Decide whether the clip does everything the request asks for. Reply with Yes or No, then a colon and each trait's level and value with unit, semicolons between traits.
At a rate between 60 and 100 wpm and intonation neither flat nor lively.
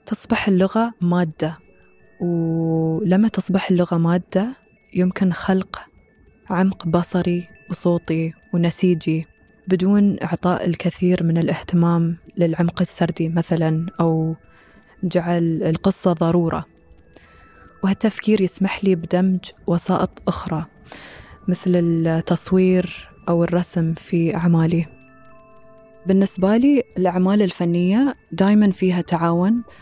No: average, 90 wpm; narrow, 2.3 semitones